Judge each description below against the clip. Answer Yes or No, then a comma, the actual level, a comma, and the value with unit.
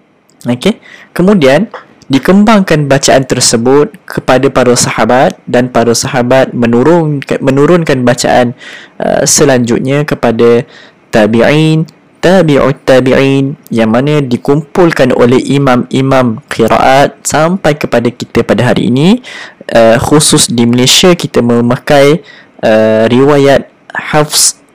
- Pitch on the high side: No, low, 135 Hz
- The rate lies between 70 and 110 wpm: Yes, average, 100 wpm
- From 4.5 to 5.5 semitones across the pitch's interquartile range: No, average, 3.9 semitones